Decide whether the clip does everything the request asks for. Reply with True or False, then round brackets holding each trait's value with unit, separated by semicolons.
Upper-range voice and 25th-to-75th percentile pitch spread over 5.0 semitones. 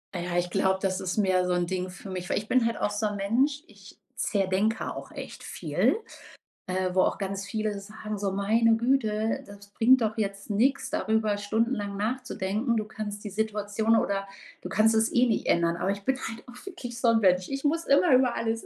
False (210 Hz; 2.7 semitones)